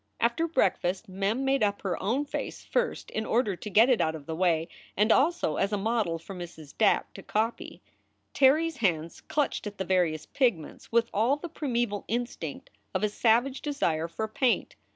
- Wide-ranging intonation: Yes, wide, 5.8 semitones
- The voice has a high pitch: Yes, high, 215 Hz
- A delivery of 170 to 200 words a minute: Yes, average, 190 wpm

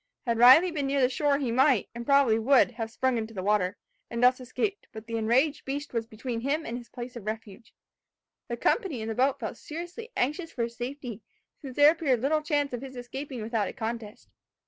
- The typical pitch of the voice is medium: No, very high, 250 Hz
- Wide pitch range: No, average, 3.6 semitones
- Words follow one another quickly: Yes, fast, 215 wpm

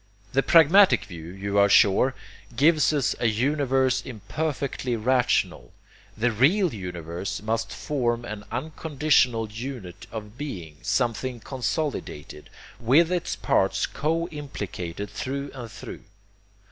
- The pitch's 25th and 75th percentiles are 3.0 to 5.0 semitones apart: No, wide, 5.6 semitones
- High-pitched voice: No, low, 125 Hz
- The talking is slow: Yes, slow, 115 wpm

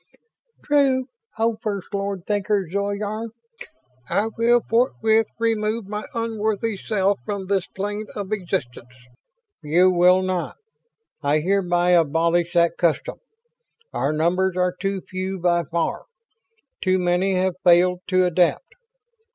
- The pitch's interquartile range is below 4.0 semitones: Yes, average, 3.1 semitones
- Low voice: No, high, 190 Hz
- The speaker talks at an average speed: No, slow, 120 wpm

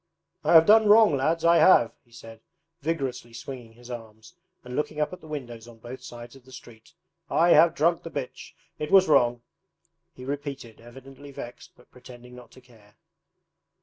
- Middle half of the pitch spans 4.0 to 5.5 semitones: Yes, average, 4.3 semitones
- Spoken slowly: No, average, 180 wpm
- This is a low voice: Yes, low, 130 Hz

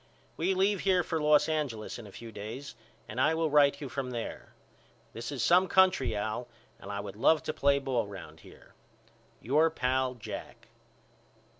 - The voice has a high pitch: No, low, 135 Hz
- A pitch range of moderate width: No, wide, 5.7 semitones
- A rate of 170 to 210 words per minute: Yes, average, 175 wpm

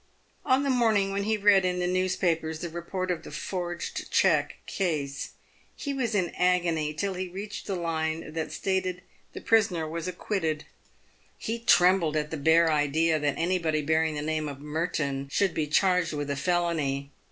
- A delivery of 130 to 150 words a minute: No, average, 185 wpm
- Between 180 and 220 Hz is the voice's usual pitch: No, medium, 170 Hz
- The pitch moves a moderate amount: Yes, average, 3.3 semitones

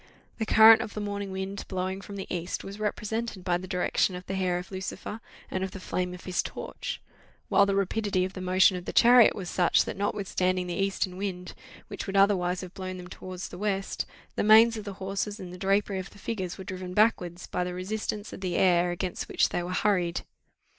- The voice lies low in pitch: No, high, 190 Hz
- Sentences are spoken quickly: Yes, fast, 220 wpm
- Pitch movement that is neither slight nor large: No, narrow, 1.9 semitones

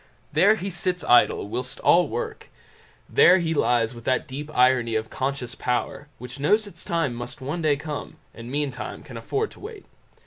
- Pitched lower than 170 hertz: Yes, medium, 140 Hz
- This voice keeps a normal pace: Yes, average, 180 wpm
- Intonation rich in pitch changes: Yes, wide, 5.8 semitones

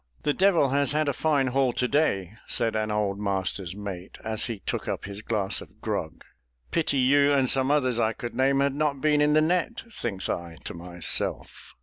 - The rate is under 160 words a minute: No, fast, 205 wpm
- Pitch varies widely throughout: Yes, wide, 6.1 semitones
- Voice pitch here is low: Yes, low, 130 Hz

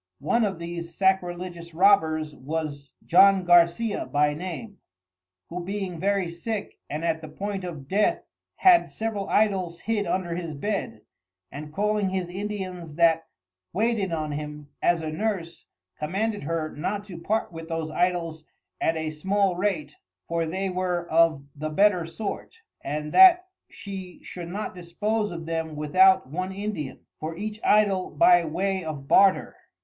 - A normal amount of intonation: Yes, average, 3.7 semitones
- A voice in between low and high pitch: Yes, medium, 175 Hz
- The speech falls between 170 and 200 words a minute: No, average, 150 wpm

